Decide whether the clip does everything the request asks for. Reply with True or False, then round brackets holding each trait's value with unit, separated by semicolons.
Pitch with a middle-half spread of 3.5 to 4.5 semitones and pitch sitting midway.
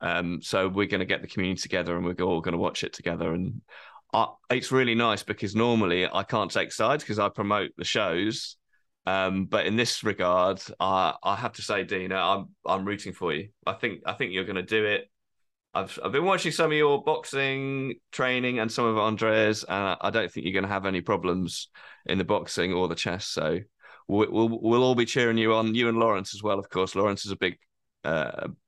False (3.8 semitones; 105 Hz)